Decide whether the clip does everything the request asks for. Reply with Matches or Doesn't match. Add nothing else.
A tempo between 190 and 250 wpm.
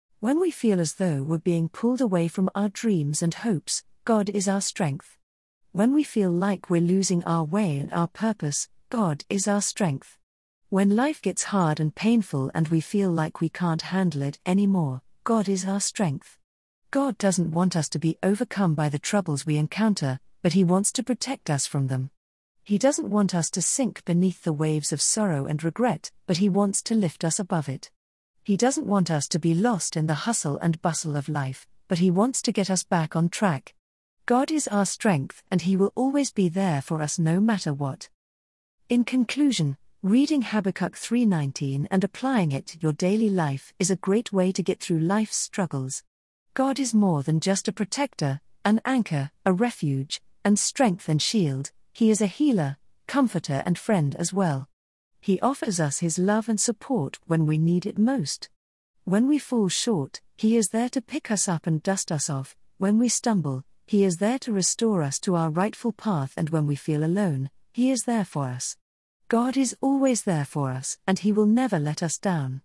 Matches